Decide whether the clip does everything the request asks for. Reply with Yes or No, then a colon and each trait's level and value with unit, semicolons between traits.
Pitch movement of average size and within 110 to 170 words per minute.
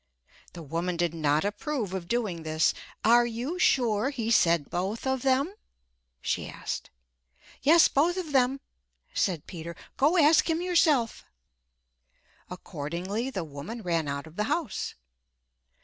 No: wide, 8.1 semitones; slow, 135 wpm